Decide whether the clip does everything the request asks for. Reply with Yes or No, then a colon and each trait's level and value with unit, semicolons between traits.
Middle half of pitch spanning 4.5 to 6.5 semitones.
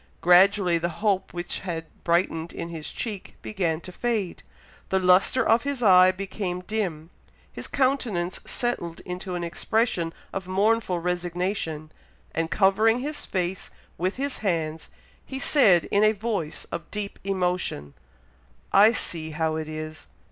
No: average, 3.9 semitones